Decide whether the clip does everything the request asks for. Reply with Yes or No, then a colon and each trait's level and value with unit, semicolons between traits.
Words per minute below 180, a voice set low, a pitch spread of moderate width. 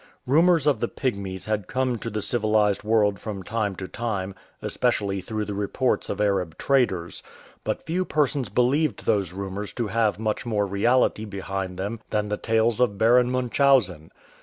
Yes: average, 165 wpm; low, 110 Hz; average, 3.8 semitones